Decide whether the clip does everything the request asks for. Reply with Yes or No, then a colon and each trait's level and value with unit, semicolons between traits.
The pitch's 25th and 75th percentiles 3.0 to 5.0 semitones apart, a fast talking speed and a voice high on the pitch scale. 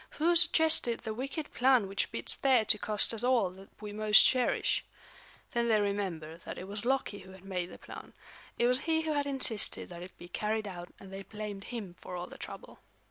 Yes: average, 4.7 semitones; fast, 215 wpm; high, 215 Hz